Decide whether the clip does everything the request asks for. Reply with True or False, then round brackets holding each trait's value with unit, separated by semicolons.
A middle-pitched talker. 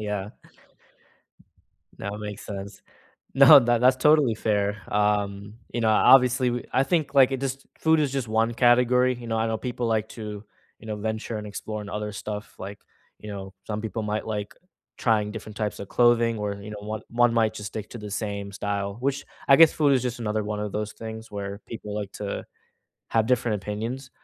False (110 Hz)